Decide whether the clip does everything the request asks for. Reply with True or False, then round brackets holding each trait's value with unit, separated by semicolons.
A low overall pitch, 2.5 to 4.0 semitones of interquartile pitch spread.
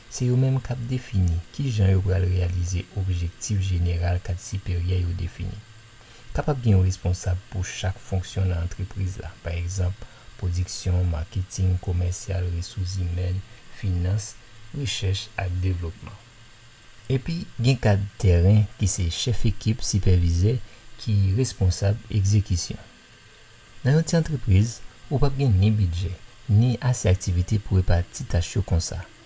True (100 Hz; 3.7 semitones)